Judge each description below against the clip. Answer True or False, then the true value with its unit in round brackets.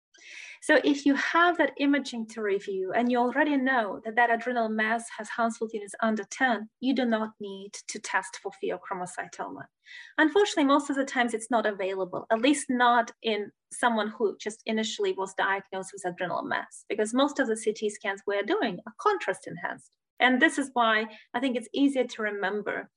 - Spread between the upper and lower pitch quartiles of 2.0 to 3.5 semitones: False (4.2 semitones)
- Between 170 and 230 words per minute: True (185 wpm)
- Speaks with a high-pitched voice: True (230 Hz)